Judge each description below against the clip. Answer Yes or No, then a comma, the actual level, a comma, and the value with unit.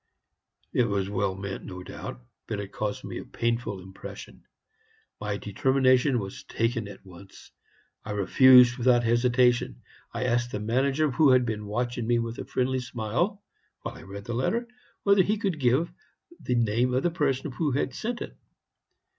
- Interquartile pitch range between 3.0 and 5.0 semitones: Yes, average, 4.0 semitones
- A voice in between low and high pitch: No, low, 120 Hz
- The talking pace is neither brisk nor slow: Yes, average, 170 wpm